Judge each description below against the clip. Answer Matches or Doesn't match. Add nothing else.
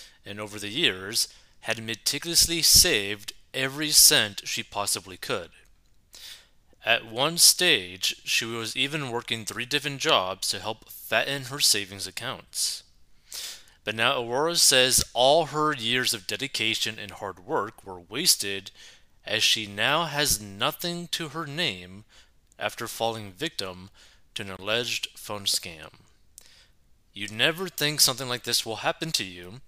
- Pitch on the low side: Matches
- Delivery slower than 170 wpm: Matches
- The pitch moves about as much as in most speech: Doesn't match